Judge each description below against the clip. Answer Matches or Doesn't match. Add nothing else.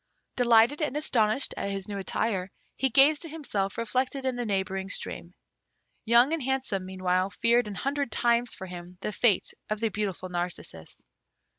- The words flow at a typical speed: Matches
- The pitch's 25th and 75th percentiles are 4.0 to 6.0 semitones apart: Matches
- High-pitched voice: Matches